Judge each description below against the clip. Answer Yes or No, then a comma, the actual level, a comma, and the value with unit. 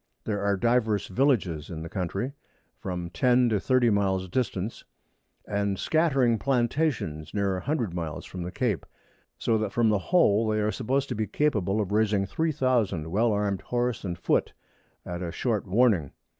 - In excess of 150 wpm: Yes, average, 170 wpm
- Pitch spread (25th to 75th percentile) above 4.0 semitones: Yes, average, 4.7 semitones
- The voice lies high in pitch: No, low, 105 Hz